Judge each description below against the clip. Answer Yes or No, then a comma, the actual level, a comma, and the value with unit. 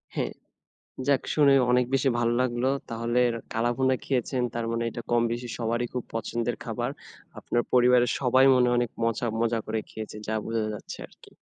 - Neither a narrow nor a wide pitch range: No, narrow, 1.4 semitones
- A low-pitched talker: Yes, low, 120 Hz